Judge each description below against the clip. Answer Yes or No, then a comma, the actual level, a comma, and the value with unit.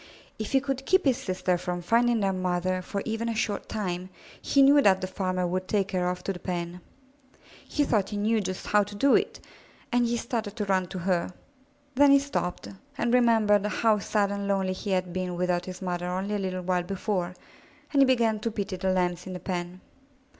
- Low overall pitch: No, high, 195 Hz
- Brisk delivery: Yes, fast, 215 wpm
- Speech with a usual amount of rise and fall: Yes, average, 3.6 semitones